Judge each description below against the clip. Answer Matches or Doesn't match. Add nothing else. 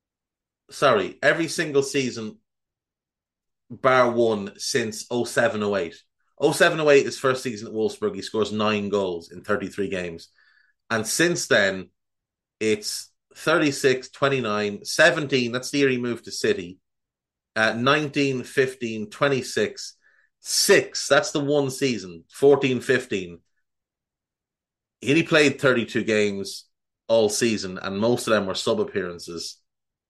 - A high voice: Doesn't match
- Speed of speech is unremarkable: Doesn't match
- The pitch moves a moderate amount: Doesn't match